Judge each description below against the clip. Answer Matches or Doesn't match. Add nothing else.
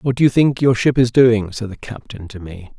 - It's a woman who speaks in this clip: Doesn't match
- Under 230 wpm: Doesn't match